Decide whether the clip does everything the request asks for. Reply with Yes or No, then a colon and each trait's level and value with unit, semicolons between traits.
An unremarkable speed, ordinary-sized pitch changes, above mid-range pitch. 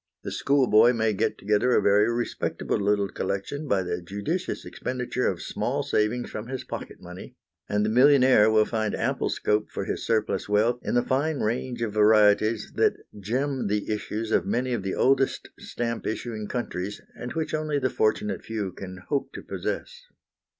No: average, 175 wpm; average, 3.5 semitones; low, 110 Hz